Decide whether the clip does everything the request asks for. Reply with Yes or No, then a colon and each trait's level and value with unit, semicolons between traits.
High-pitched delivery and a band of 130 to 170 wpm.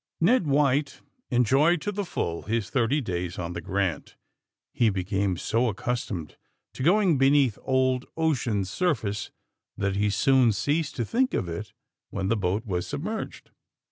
No: low, 120 Hz; average, 160 wpm